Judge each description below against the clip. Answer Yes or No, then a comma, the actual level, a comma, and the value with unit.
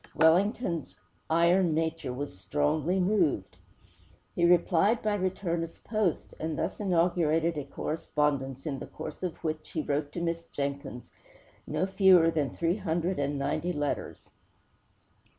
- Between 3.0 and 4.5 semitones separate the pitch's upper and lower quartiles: Yes, average, 3.4 semitones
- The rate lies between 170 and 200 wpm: No, slow, 135 wpm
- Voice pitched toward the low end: No, medium, 165 Hz